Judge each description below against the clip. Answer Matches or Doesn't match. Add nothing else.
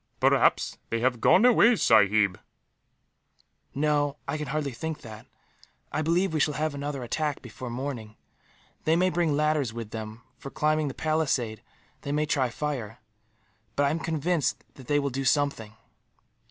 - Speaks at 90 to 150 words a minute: Doesn't match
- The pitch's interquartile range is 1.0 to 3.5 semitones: Doesn't match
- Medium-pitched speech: Matches